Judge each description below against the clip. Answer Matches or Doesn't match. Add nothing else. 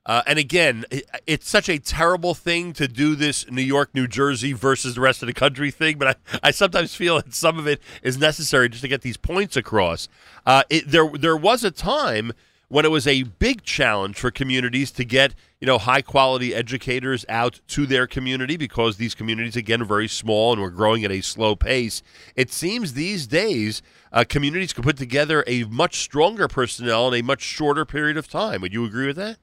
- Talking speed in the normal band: Doesn't match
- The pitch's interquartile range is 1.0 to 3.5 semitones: Doesn't match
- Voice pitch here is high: Doesn't match